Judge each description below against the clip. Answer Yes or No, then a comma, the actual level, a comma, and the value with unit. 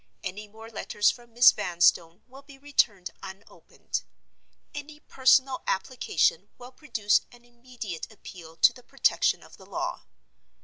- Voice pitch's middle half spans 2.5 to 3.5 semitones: No, average, 5.2 semitones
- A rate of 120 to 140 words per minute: Yes, slow, 135 wpm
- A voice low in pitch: No, high, 230 Hz